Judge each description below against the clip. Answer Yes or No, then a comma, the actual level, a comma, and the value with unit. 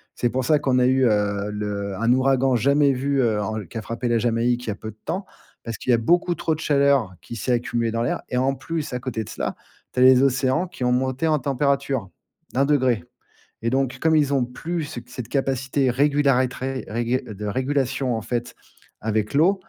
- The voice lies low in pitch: Yes, low, 130 Hz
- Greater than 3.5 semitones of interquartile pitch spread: No, average, 3.1 semitones